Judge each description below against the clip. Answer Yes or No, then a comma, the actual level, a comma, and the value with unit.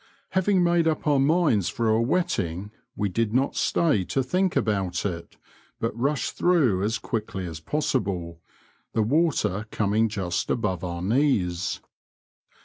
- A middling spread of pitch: No, wide, 7.6 semitones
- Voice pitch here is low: Yes, low, 110 Hz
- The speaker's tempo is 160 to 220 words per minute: No, average, 140 wpm